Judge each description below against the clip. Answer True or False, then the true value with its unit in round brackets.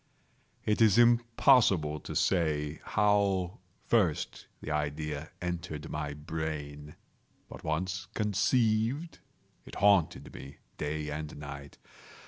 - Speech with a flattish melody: False (5.5 semitones)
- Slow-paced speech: True (105 wpm)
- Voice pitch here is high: False (80 Hz)